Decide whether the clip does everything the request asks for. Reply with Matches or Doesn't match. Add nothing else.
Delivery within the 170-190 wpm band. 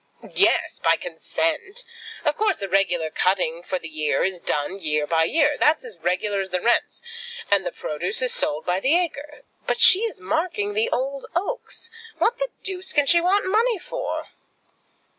Matches